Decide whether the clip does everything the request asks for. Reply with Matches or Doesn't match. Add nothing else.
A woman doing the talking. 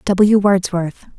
Matches